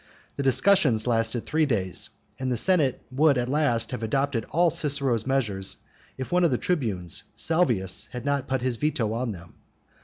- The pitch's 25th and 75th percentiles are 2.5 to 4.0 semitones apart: No, average, 4.5 semitones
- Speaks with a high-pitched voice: No, low, 130 Hz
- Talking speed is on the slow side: No, average, 175 wpm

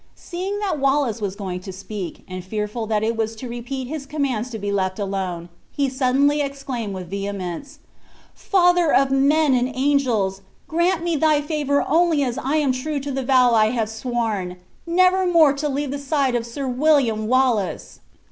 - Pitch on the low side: No, very high, 260 Hz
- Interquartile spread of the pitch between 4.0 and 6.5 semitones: Yes, average, 5.2 semitones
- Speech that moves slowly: No, average, 180 wpm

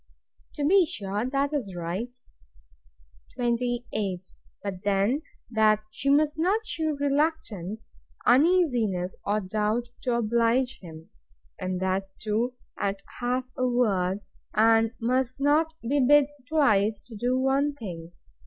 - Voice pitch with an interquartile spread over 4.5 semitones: Yes, wide, 5.5 semitones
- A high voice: Yes, high, 235 Hz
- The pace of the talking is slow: Yes, slow, 125 wpm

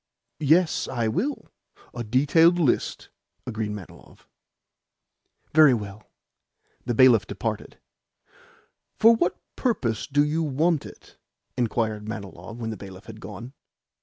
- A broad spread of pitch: Yes, wide, 6.2 semitones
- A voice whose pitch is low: Yes, low, 120 Hz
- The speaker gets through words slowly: Yes, slow, 115 wpm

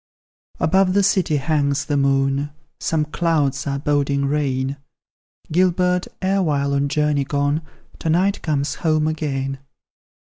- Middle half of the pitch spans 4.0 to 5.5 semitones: No, average, 2.7 semitones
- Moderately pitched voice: Yes, medium, 150 Hz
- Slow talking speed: Yes, slow, 125 wpm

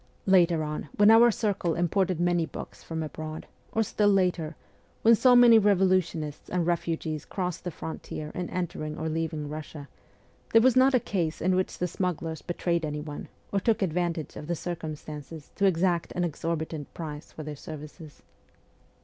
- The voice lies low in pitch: No, medium, 170 Hz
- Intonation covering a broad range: No, average, 3.2 semitones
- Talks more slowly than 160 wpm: No, average, 165 wpm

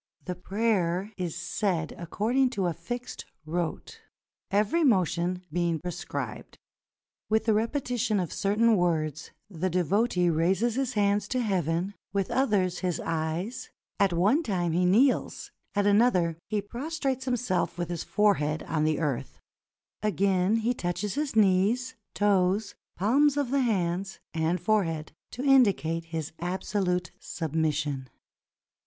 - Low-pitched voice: No, high, 190 Hz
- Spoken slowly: Yes, slow, 130 wpm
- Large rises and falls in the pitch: No, average, 4.5 semitones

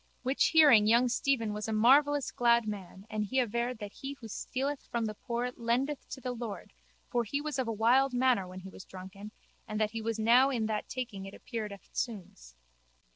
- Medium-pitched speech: No, high, 230 Hz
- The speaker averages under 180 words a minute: No, fast, 205 wpm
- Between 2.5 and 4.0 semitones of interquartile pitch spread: Yes, average, 3.4 semitones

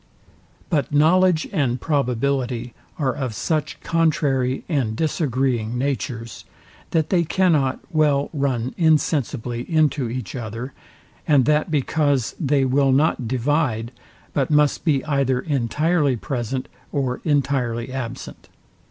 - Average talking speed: No, slow, 115 wpm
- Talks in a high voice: No, medium, 140 Hz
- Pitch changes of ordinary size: Yes, average, 3.3 semitones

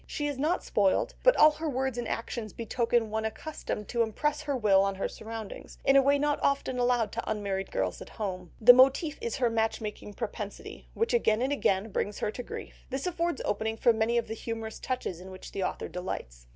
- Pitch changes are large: No, average, 4.7 semitones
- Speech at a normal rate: No, fast, 220 wpm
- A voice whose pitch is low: No, high, 230 Hz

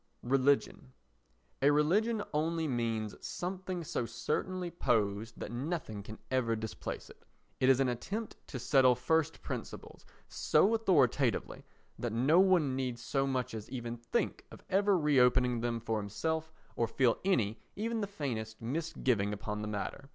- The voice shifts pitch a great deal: Yes, wide, 5.9 semitones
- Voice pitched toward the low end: Yes, low, 130 Hz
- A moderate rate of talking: Yes, average, 150 wpm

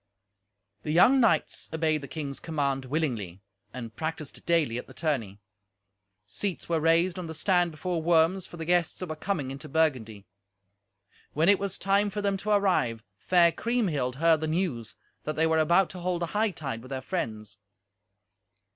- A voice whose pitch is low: No, medium, 160 Hz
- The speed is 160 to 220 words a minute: Yes, average, 175 wpm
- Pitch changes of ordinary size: Yes, average, 4.8 semitones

